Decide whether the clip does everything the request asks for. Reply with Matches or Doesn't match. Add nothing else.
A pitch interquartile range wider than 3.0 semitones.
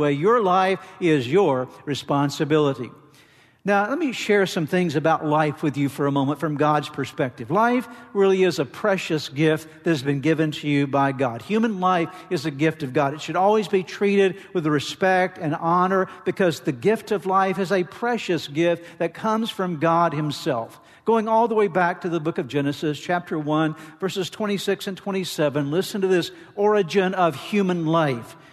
Matches